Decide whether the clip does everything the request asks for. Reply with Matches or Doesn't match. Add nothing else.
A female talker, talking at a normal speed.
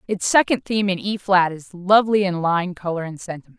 Doesn't match